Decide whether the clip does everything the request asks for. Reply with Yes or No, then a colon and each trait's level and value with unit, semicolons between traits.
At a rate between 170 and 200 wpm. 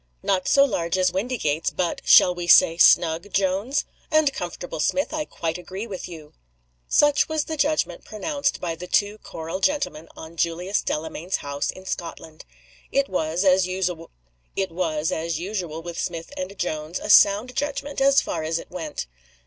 No: average, 155 wpm